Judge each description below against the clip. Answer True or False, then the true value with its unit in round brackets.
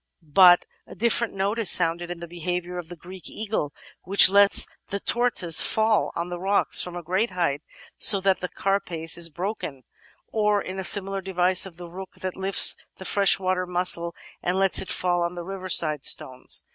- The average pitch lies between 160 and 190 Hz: True (185 Hz)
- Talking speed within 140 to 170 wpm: False (185 wpm)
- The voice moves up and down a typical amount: False (2.1 semitones)